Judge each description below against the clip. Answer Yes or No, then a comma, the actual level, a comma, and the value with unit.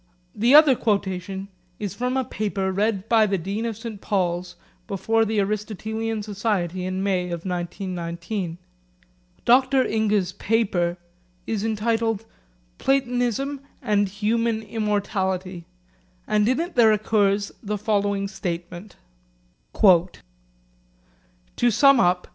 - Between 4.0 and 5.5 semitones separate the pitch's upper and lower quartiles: No, average, 3.5 semitones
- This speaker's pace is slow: Yes, slow, 115 wpm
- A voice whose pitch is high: Yes, high, 205 Hz